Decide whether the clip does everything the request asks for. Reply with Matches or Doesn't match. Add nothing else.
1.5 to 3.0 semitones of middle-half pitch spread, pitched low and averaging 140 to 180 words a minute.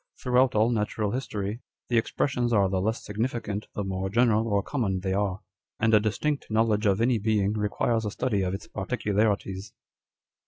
Matches